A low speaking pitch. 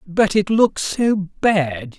No: high, 190 Hz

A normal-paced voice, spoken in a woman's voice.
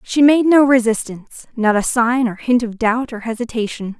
Yes: average, 195 wpm; female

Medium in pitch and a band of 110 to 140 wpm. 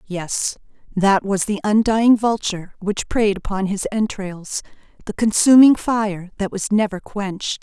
No: high, 205 Hz; slow, 135 wpm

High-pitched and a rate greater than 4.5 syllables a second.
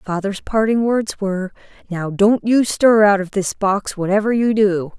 No: high, 205 Hz; 4.4 syllables/s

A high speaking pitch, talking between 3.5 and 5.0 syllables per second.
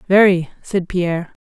No: medium, 180 Hz; 4.7 syllables/s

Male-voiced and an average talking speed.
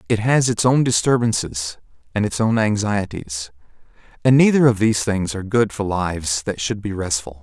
Yes: male; average, 180 wpm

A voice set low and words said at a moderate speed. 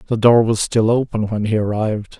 No: low, 110 Hz; fast, 220 wpm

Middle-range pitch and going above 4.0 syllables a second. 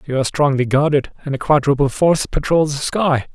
Yes: medium, 145 Hz; 6.0 syllables/s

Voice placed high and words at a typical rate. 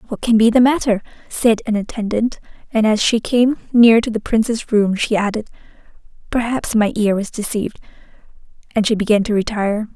Yes: high, 220 Hz; average, 175 wpm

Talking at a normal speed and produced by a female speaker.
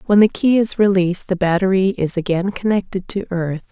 Yes: average, 195 wpm; female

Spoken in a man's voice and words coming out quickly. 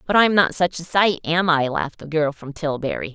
No: female; fast, 250 wpm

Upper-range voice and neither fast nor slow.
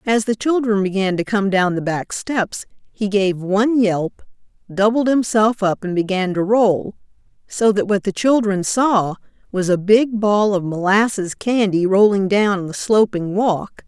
Yes: high, 205 Hz; average, 170 wpm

